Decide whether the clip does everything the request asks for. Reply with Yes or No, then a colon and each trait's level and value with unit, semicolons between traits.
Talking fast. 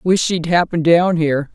No: average, 195 wpm